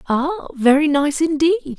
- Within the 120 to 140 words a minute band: Yes, slow, 135 wpm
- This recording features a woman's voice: Yes, female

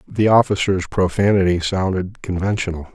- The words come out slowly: Yes, slow, 100 wpm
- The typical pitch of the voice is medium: No, very low, 95 Hz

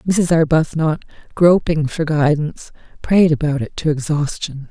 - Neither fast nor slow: No, slow, 125 wpm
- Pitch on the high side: No, medium, 155 Hz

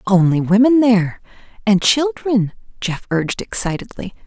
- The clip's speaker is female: Yes, female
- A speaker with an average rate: No, slow, 100 wpm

